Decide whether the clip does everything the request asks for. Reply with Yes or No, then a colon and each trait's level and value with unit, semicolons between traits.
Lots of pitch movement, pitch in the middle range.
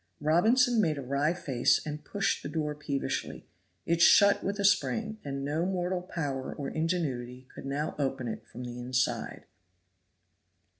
No: average, 4.8 semitones; medium, 150 Hz